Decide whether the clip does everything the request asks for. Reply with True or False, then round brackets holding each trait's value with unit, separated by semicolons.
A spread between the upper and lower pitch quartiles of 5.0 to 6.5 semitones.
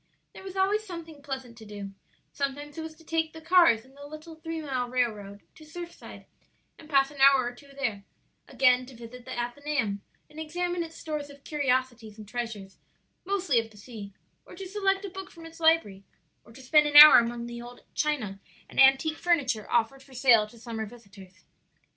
True (5.4 semitones)